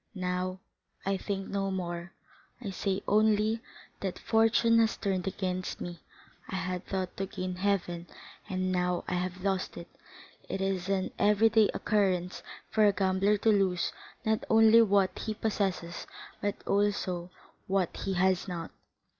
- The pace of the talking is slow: No, average, 145 wpm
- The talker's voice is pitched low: No, high, 195 Hz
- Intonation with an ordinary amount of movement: No, narrow, 2.2 semitones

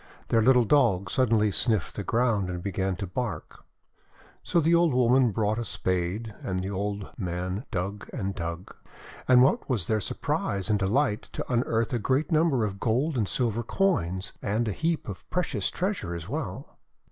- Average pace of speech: Yes, average, 180 wpm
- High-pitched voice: No, low, 110 Hz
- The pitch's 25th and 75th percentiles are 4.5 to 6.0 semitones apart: Yes, average, 4.9 semitones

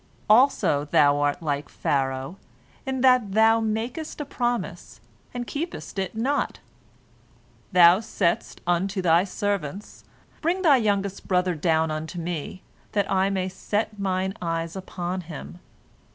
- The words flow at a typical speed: No, slow, 130 wpm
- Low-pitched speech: No, high, 190 Hz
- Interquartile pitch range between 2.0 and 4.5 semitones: No, average, 5.0 semitones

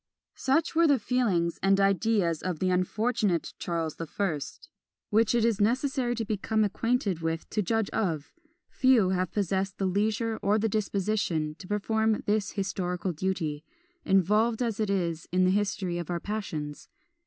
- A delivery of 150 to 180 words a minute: Yes, average, 165 wpm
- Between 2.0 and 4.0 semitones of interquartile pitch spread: Yes, average, 3.7 semitones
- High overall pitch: Yes, high, 200 Hz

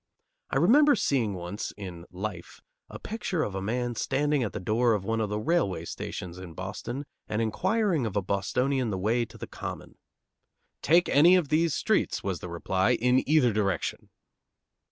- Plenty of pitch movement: Yes, wide, 7.2 semitones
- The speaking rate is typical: Yes, average, 175 wpm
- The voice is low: Yes, low, 115 Hz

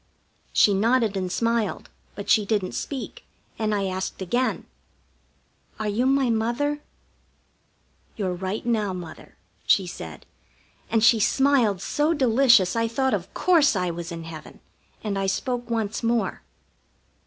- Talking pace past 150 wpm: No, average, 140 wpm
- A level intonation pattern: No, average, 4.3 semitones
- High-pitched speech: Yes, high, 220 Hz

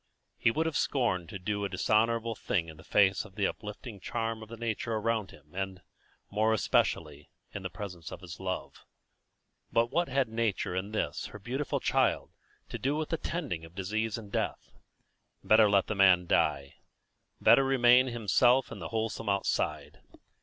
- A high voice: No, low, 110 Hz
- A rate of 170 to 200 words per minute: Yes, average, 175 wpm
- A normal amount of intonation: Yes, average, 3.6 semitones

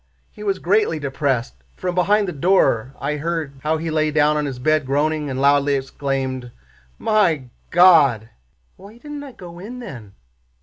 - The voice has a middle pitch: Yes, medium, 155 Hz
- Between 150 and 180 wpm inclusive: Yes, average, 165 wpm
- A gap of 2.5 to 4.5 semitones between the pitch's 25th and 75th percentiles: No, average, 5.0 semitones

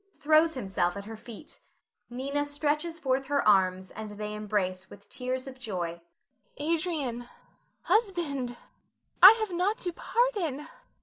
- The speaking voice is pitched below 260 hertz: No, very high, 265 Hz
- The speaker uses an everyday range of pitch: No, wide, 7.1 semitones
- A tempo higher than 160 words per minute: No, slow, 135 wpm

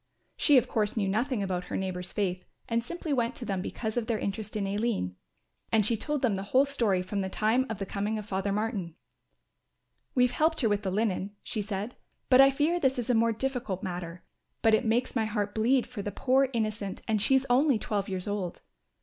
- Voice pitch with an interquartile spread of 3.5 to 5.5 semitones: Yes, average, 3.9 semitones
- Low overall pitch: No, high, 215 Hz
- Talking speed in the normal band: No, fast, 220 wpm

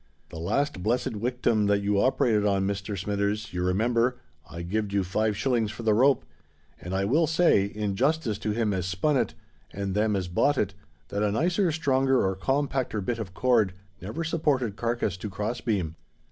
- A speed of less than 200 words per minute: Yes, average, 190 wpm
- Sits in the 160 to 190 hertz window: No, low, 105 Hz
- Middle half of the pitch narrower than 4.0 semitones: No, average, 4.4 semitones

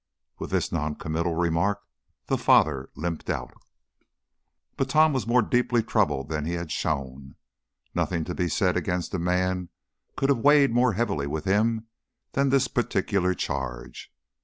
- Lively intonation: Yes, wide, 7.2 semitones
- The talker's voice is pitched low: Yes, very low, 90 Hz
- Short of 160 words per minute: Yes, average, 150 wpm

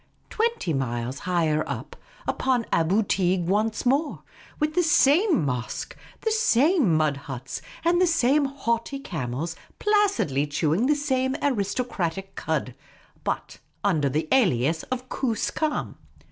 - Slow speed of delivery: Yes, slow, 130 wpm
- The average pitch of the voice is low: No, high, 215 Hz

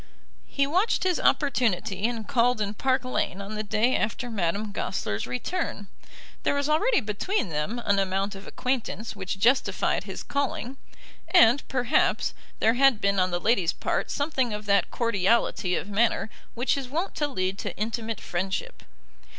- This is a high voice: Yes, high, 225 Hz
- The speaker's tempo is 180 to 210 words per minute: No, average, 160 wpm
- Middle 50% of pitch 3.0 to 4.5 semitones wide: No, average, 5.0 semitones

